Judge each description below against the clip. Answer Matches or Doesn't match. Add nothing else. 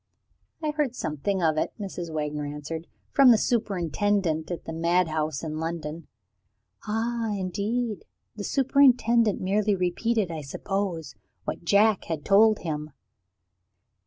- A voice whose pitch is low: Doesn't match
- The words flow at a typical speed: Doesn't match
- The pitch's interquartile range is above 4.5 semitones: Matches